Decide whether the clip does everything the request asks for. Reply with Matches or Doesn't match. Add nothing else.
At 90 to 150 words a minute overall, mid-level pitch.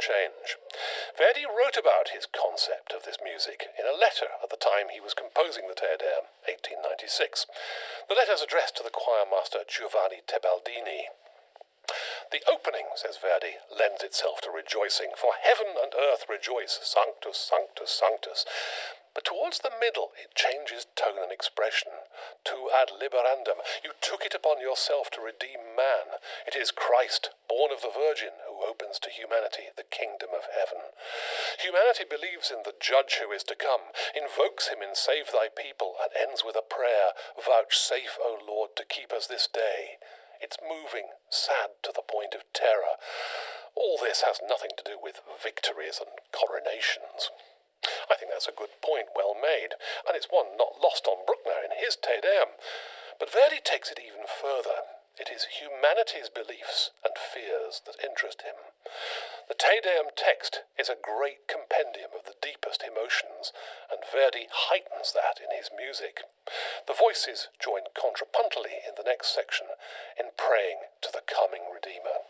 Doesn't match